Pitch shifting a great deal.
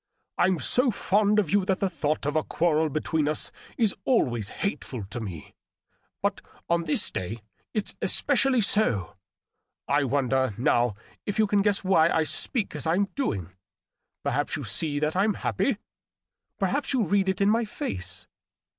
Yes: wide, 7.4 semitones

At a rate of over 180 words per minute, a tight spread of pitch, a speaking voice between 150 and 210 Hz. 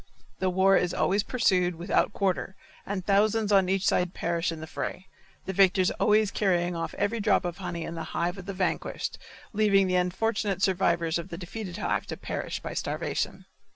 Yes: average, 190 wpm; narrow, 2.3 semitones; high, 190 Hz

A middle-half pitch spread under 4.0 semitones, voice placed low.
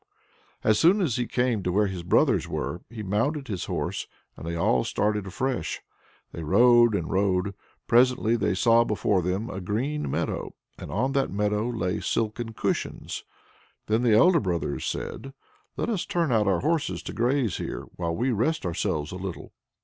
No: average, 5.1 semitones; low, 110 Hz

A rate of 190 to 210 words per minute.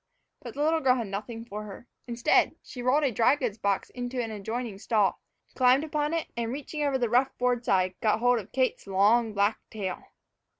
Yes: fast, 205 wpm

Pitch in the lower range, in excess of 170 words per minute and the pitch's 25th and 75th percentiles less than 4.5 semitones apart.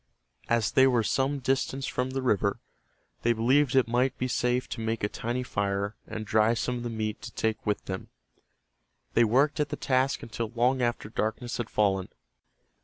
Yes: low, 120 Hz; average, 185 wpm; average, 2.9 semitones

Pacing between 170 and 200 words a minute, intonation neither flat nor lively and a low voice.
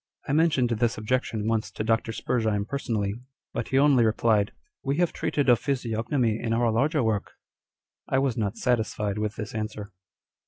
Yes: average, 185 wpm; average, 3.3 semitones; low, 115 Hz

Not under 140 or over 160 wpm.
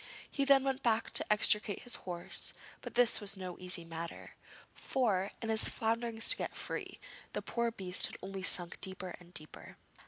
No: average, 180 wpm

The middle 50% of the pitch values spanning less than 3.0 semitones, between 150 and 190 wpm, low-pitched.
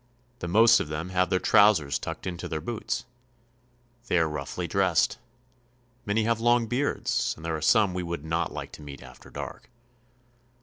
No: wide, 5.5 semitones; average, 175 wpm; very low, 90 Hz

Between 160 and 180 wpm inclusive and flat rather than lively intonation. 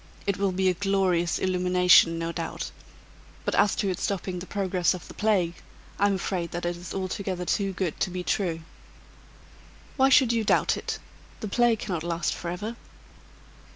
Yes: average, 175 wpm; narrow, 2.3 semitones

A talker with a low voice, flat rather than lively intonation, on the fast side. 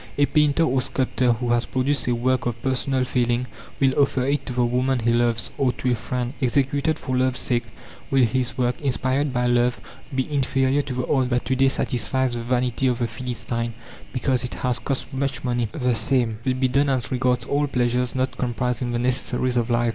Yes: low, 125 Hz; narrow, 1.5 semitones; fast, 210 wpm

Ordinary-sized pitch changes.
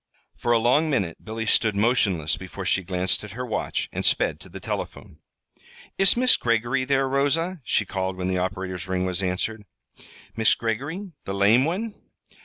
No: wide, 6.4 semitones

